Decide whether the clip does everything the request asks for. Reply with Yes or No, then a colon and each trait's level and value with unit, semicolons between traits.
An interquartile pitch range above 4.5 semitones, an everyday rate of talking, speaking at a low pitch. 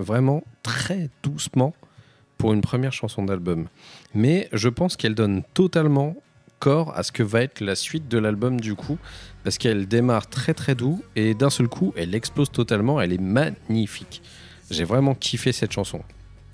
Yes: average, 5.2 semitones; average, 170 wpm; low, 120 Hz